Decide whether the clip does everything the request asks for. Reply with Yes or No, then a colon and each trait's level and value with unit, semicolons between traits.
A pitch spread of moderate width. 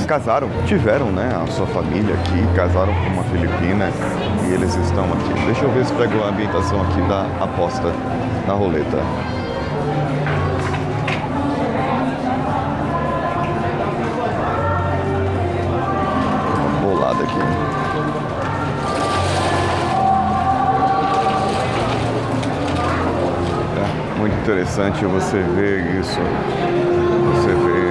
Yes: average, 3.0 semitones